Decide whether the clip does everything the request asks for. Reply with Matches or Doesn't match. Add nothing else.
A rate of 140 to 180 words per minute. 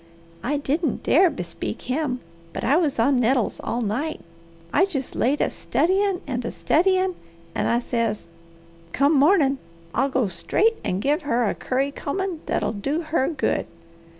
Matches